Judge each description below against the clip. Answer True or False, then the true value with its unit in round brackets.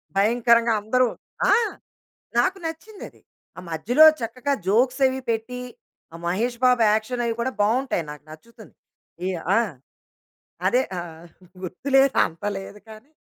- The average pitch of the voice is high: True (235 Hz)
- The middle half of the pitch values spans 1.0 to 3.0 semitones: False (4.0 semitones)